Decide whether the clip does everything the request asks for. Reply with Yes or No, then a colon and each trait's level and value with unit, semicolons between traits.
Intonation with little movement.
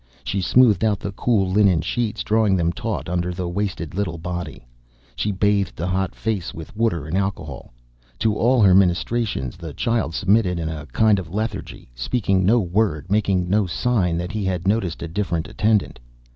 No: average, 3.7 semitones